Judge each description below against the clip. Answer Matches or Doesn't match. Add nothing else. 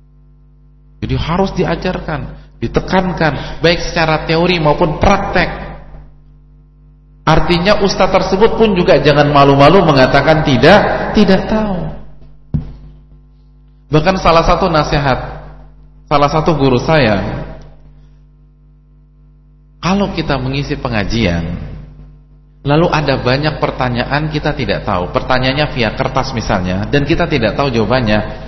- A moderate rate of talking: Doesn't match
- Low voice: Doesn't match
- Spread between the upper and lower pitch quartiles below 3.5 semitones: Matches